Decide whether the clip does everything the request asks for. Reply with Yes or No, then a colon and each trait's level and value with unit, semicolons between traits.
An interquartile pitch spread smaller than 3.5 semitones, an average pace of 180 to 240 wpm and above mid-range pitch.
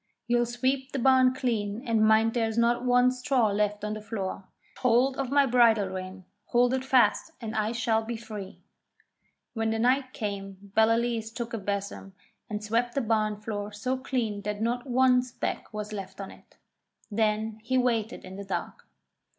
Yes: average, 2.9 semitones; average, 185 wpm; high, 225 Hz